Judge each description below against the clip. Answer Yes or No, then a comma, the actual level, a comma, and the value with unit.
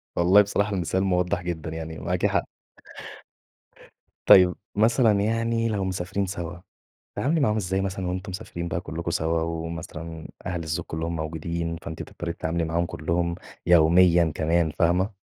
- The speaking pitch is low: Yes, very low, 85 Hz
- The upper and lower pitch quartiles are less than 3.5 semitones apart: Yes, narrow, 2.5 semitones